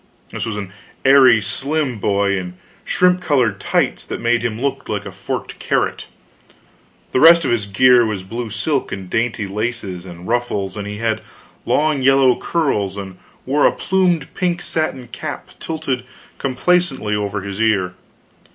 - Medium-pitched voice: No, low, 120 Hz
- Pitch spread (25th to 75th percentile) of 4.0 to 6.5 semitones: Yes, average, 5.2 semitones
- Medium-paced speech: Yes, average, 160 wpm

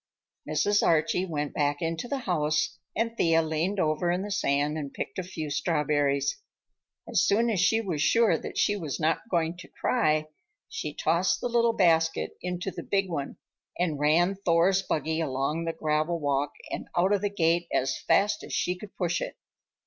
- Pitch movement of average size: Yes, average, 3.8 semitones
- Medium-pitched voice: Yes, medium, 165 Hz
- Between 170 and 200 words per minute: Yes, average, 185 wpm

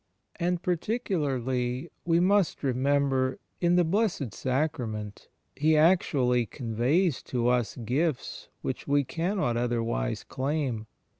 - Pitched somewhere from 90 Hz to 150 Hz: Yes, medium, 140 Hz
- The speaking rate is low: Yes, slow, 105 wpm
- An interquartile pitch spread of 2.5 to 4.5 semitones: No, wide, 5.5 semitones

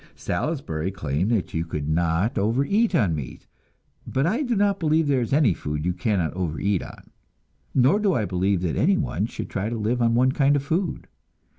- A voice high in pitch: No, low, 110 Hz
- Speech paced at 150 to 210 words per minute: Yes, average, 190 wpm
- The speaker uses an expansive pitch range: Yes, wide, 8.6 semitones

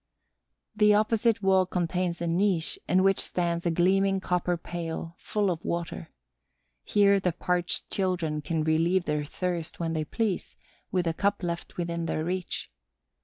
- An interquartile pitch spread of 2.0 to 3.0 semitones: Yes, narrow, 2.5 semitones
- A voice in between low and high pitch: Yes, medium, 175 Hz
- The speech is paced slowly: No, average, 155 wpm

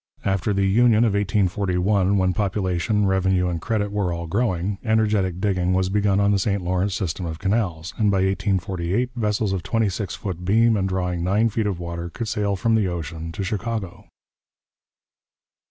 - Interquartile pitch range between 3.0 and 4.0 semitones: No, narrow, 2.5 semitones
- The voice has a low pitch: Yes, very low, 95 Hz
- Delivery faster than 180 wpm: No, average, 175 wpm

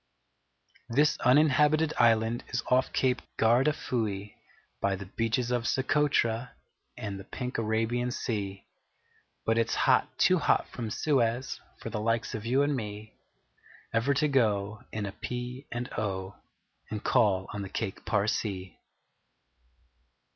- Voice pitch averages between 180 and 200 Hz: No, low, 115 Hz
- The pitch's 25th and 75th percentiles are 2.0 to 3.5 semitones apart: Yes, average, 3.2 semitones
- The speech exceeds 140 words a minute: No, slow, 135 wpm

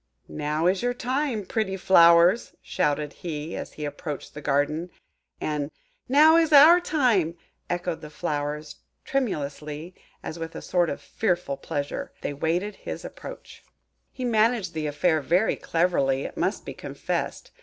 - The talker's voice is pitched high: No, medium, 170 Hz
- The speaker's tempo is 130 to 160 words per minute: Yes, average, 145 wpm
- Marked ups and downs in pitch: Yes, wide, 6.4 semitones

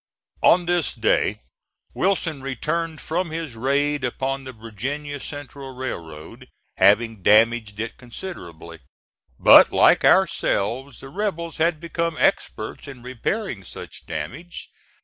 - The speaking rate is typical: No, slow, 115 wpm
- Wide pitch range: Yes, wide, 6.3 semitones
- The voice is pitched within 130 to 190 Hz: Yes, low, 135 Hz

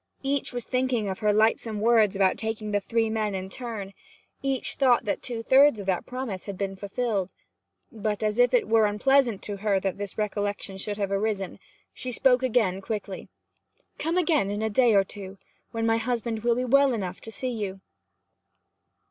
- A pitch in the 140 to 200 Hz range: No, high, 220 Hz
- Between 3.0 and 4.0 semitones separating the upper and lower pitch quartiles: Yes, average, 3.5 semitones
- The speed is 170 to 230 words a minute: Yes, average, 190 wpm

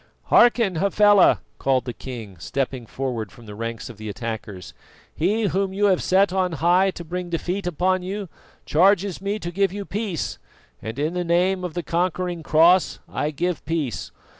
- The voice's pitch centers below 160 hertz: No, medium, 175 Hz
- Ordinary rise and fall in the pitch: No, wide, 6.0 semitones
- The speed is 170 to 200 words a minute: Yes, average, 175 wpm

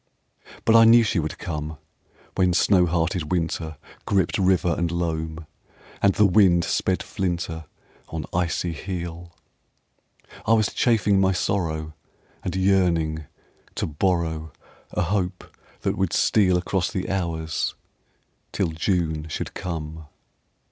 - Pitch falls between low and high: No, very low, 85 Hz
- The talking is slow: Yes, slow, 125 wpm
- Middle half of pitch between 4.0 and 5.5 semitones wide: No, average, 2.8 semitones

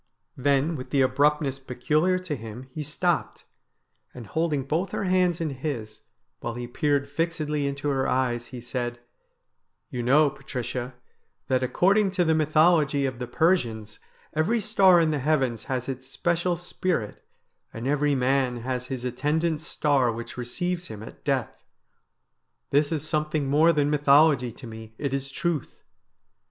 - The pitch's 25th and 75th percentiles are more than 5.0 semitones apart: No, average, 4.0 semitones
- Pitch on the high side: No, medium, 140 Hz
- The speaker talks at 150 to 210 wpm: Yes, average, 160 wpm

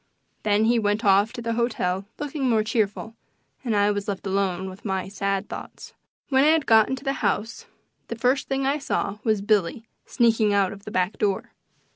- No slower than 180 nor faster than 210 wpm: Yes, average, 190 wpm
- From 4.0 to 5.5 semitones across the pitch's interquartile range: No, average, 3.1 semitones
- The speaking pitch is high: Yes, high, 215 Hz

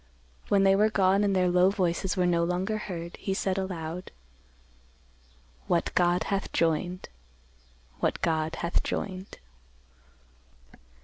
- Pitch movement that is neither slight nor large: No, narrow, 2.1 semitones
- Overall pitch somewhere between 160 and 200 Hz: Yes, medium, 185 Hz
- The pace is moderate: No, slow, 125 wpm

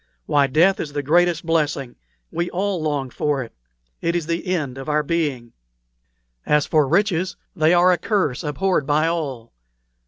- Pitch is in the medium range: Yes, medium, 155 Hz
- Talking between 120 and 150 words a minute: No, average, 165 wpm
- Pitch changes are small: No, average, 3.3 semitones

